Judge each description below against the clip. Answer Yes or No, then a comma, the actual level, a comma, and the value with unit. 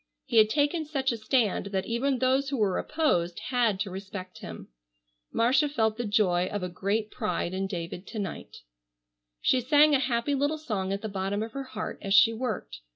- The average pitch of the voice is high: Yes, high, 220 Hz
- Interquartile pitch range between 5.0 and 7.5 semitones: Yes, average, 5.3 semitones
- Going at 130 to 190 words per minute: No, average, 200 wpm